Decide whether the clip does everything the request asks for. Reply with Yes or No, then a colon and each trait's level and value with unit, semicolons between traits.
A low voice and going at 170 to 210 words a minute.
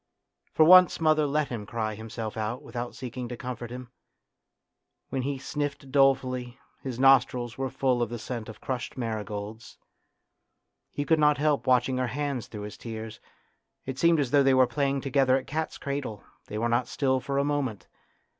Yes: low, 130 Hz; average, 180 wpm